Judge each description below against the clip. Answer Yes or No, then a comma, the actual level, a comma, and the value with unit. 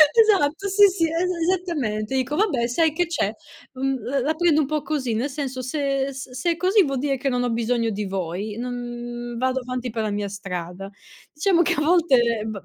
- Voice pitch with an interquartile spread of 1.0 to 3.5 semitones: No, average, 5.0 semitones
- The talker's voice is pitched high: Yes, very high, 260 Hz